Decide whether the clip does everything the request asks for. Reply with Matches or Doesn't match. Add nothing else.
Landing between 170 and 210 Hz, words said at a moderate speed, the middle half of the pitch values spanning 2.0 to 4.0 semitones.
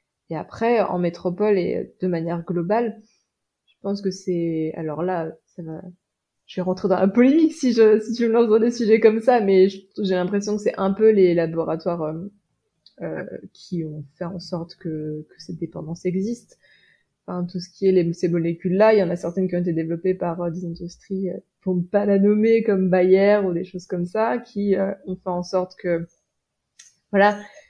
Matches